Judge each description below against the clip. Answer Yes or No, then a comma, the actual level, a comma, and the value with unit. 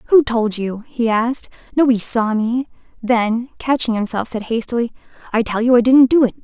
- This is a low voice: No, high, 235 Hz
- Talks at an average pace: Yes, average, 185 wpm